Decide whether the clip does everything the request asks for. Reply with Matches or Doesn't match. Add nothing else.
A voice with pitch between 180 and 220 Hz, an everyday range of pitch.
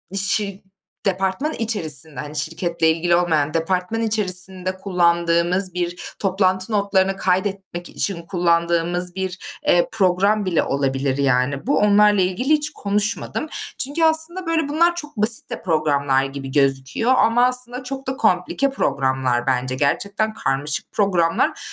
Matches